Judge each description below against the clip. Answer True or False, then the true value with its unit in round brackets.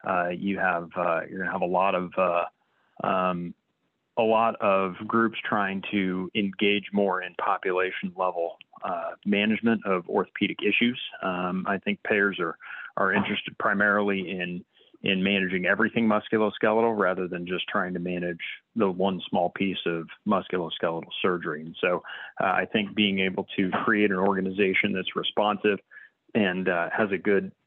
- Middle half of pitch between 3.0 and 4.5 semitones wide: False (2.4 semitones)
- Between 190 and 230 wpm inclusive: False (160 wpm)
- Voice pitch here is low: True (95 Hz)